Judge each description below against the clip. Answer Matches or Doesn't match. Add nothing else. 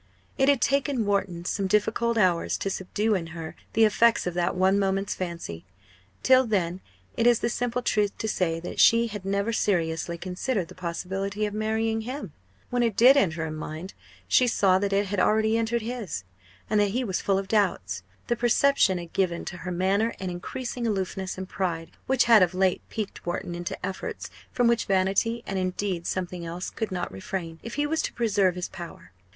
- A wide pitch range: Doesn't match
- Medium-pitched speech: Doesn't match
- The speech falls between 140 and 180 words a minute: Doesn't match